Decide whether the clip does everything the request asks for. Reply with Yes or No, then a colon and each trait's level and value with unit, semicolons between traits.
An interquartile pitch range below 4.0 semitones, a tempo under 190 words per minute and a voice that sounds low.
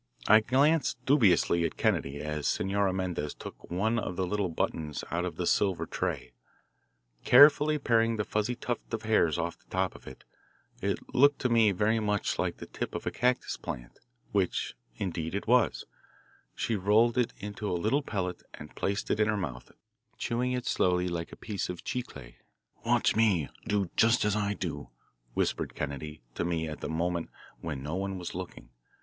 No: average, 5.0 semitones; average, 180 wpm; low, 100 Hz